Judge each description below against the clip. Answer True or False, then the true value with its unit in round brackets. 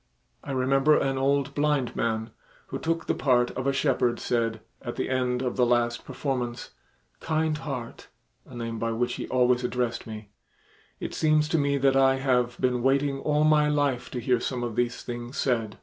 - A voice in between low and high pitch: False (130 Hz)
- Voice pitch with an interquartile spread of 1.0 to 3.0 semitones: True (2.6 semitones)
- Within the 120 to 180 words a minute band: False (190 wpm)